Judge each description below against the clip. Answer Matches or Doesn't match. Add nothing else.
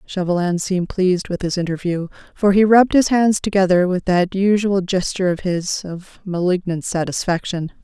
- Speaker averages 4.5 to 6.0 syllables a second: Matches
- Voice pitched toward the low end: Doesn't match